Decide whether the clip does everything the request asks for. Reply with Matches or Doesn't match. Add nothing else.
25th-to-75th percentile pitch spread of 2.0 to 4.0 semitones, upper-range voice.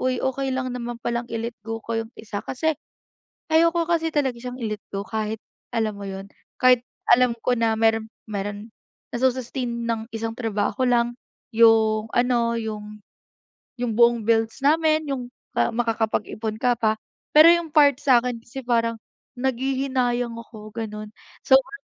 Matches